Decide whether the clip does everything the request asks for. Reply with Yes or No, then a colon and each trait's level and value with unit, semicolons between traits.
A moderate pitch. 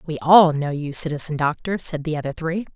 Yes: medium, 160 Hz